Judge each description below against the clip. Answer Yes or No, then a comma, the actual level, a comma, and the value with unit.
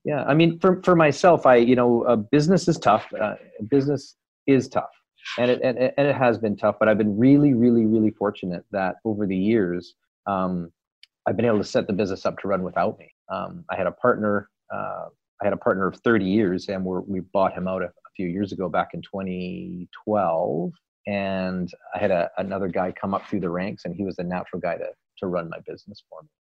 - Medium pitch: No, low, 105 Hz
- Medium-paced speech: No, fast, 225 wpm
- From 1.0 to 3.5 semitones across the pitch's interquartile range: No, wide, 5.4 semitones